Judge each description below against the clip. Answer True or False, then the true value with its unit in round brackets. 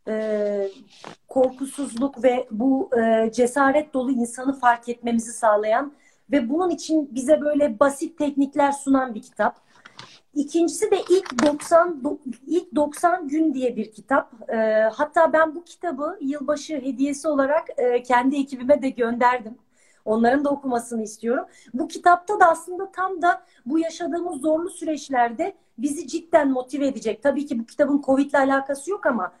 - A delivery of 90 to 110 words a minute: False (135 wpm)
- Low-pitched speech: False (280 Hz)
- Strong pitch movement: False (4.4 semitones)